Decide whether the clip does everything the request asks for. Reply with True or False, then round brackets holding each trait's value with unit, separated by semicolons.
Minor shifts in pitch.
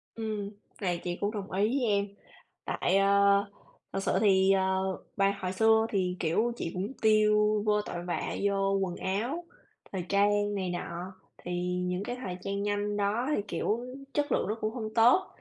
True (2.2 semitones)